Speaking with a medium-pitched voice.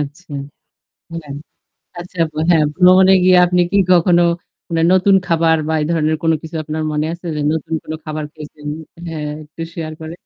Yes: medium, 160 Hz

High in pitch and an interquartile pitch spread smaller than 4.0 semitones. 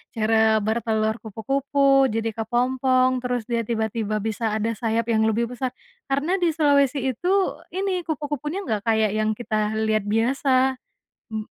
Yes: high, 235 Hz; average, 3.5 semitones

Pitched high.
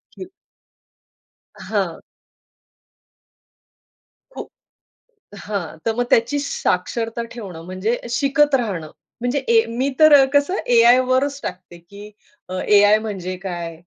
Yes: high, 225 Hz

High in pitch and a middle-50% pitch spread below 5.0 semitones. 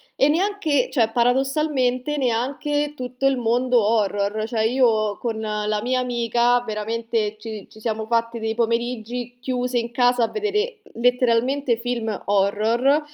Yes: high, 240 Hz; narrow, 2.4 semitones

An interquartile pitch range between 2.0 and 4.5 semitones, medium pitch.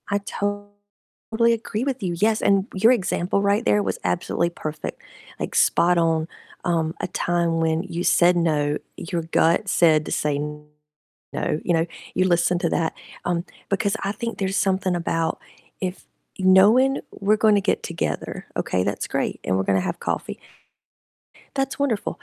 Yes: average, 3.8 semitones; medium, 180 Hz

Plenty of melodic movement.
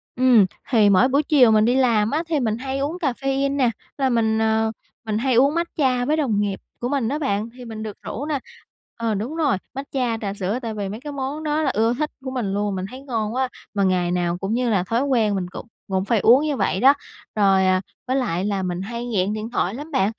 No: average, 4.7 semitones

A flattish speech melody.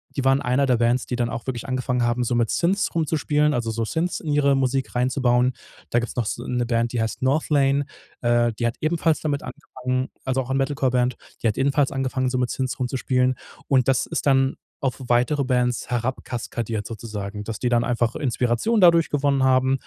Yes: narrow, 2.3 semitones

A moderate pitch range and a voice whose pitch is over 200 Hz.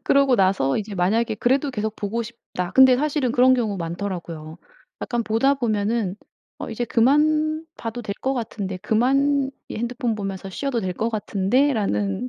Yes: average, 4.8 semitones; high, 225 Hz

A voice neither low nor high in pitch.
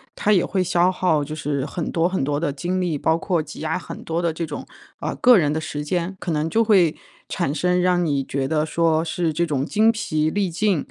Yes: medium, 165 Hz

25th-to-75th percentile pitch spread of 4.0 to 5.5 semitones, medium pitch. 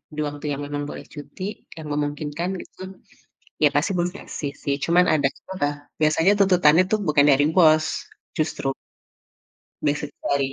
No: narrow, 2.6 semitones; medium, 150 Hz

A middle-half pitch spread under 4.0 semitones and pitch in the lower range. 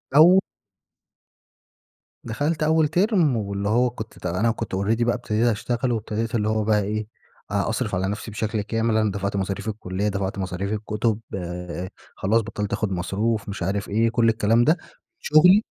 Yes: average, 2.8 semitones; low, 110 Hz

